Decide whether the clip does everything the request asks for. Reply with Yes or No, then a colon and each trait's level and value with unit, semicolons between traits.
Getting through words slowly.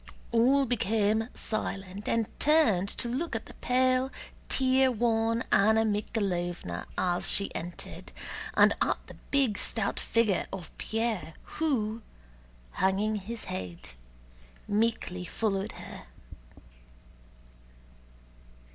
Yes: slow, 100 wpm